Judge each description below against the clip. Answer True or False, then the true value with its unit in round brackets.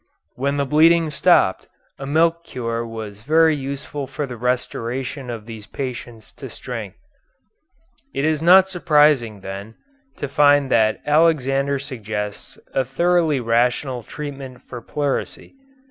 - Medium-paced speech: False (130 wpm)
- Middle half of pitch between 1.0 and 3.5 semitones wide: False (4.1 semitones)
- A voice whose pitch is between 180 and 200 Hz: False (135 Hz)